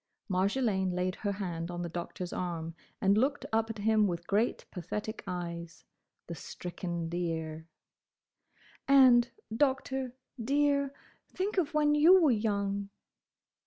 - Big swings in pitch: Yes, wide, 7.0 semitones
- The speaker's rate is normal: No, slow, 120 wpm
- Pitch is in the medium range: No, high, 200 Hz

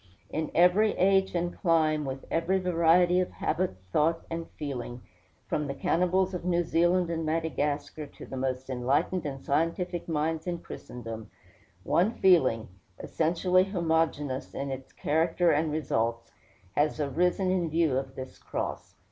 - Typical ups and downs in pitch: Yes, average, 4.1 semitones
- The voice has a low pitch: No, medium, 160 Hz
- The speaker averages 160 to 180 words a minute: No, average, 145 wpm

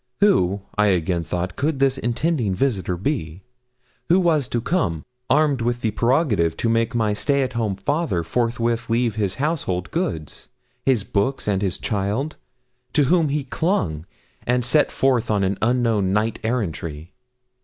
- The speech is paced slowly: No, average, 155 wpm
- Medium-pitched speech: No, low, 115 Hz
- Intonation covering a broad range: Yes, wide, 6.0 semitones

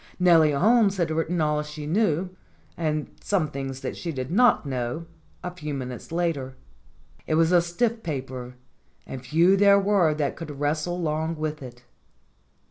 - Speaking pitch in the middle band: Yes, medium, 155 Hz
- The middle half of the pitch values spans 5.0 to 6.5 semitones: No, average, 3.9 semitones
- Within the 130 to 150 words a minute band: No, average, 165 wpm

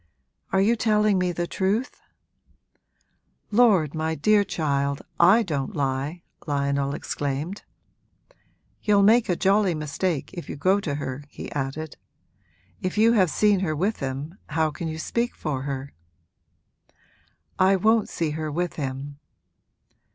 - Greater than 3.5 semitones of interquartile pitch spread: Yes, wide, 5.6 semitones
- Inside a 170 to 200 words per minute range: No, slow, 135 wpm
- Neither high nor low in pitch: Yes, medium, 165 Hz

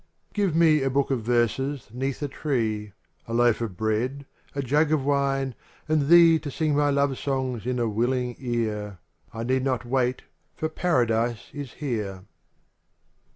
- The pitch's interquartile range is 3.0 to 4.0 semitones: Yes, average, 3.4 semitones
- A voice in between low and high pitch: No, low, 130 Hz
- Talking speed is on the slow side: No, average, 165 wpm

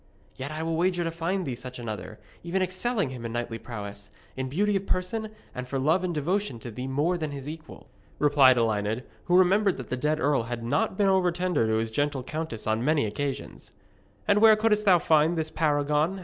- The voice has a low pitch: No, medium, 150 Hz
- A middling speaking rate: No, fast, 210 wpm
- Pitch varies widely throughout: Yes, wide, 6.3 semitones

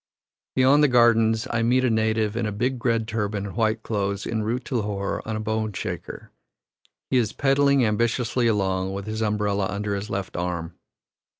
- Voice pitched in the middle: No, low, 110 Hz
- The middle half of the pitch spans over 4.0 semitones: No, narrow, 2.5 semitones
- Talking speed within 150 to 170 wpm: No, average, 185 wpm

